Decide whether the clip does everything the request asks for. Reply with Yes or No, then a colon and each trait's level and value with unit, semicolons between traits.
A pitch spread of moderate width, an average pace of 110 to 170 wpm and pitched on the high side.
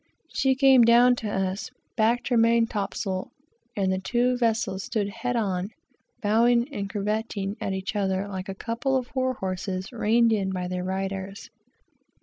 Yes: average, 3.6 semitones; average, 165 wpm; high, 210 Hz